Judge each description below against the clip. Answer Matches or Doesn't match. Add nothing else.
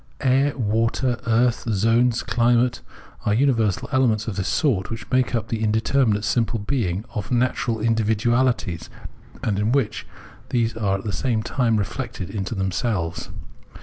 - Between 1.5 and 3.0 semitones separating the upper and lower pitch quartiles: Matches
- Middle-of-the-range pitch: Doesn't match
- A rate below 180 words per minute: Matches